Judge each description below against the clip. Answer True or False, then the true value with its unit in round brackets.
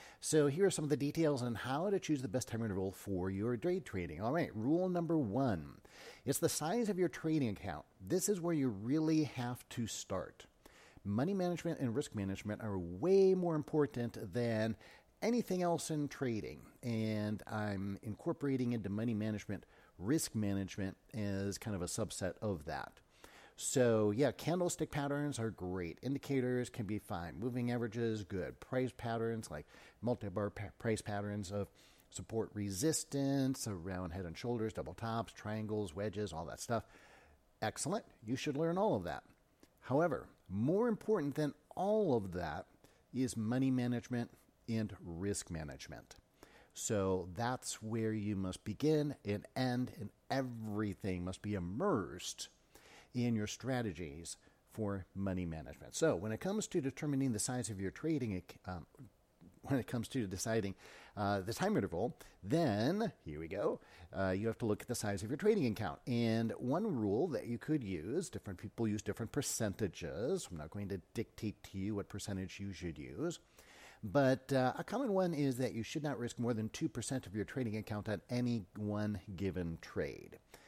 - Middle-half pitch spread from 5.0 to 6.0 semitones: True (5.3 semitones)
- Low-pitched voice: True (115 Hz)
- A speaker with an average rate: True (170 wpm)